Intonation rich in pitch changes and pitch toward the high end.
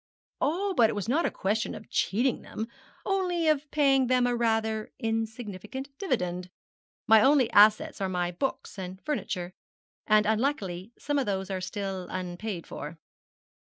Yes: wide, 6.0 semitones; high, 220 Hz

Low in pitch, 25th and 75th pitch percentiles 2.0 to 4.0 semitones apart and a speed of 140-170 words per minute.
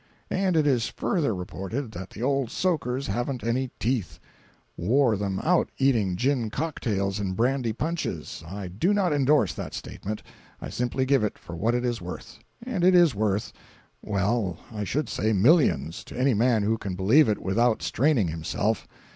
No: low, 115 Hz; wide, 5.6 semitones; average, 160 wpm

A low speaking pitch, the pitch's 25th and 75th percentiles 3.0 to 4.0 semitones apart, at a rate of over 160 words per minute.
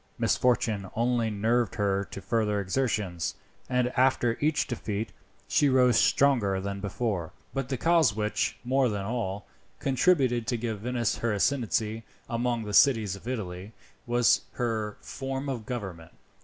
No: low, 115 Hz; average, 3.5 semitones; average, 145 wpm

